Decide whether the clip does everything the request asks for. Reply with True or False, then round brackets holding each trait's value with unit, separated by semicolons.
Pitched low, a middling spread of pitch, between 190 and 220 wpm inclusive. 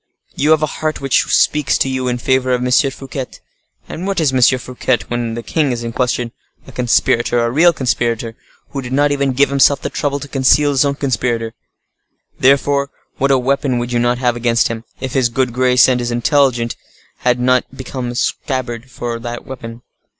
False (130 Hz; 2.3 semitones; 200 wpm)